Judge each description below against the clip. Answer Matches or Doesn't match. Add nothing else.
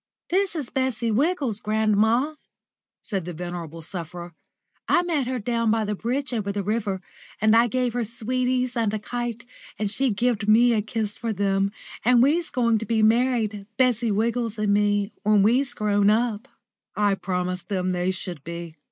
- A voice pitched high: Matches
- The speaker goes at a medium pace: Matches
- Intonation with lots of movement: Doesn't match